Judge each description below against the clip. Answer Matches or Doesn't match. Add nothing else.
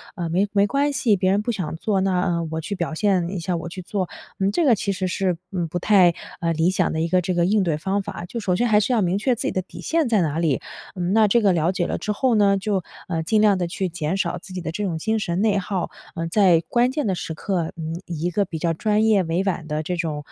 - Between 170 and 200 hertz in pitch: Matches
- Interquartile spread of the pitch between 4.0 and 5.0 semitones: Doesn't match